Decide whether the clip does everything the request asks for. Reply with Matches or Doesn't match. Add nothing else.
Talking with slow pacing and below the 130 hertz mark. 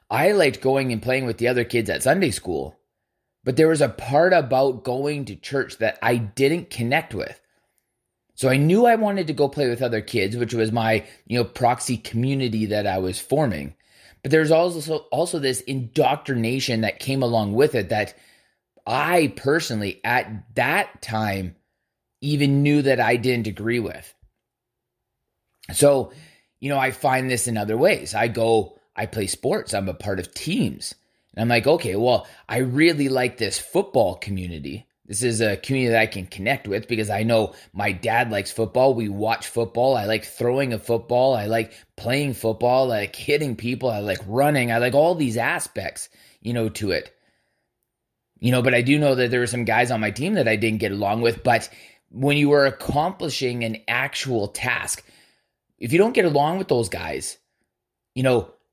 Doesn't match